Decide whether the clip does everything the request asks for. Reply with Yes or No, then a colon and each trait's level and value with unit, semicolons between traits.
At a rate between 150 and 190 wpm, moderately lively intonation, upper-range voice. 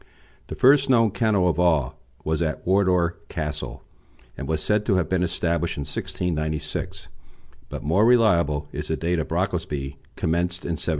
No: average, 170 wpm; average, 3.6 semitones; very low, 85 Hz